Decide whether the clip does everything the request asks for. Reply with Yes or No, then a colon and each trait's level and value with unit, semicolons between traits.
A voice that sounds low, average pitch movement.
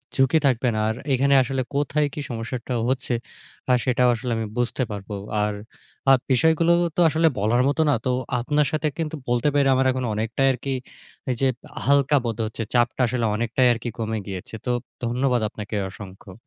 Yes: low, 125 Hz; average, 3.3 semitones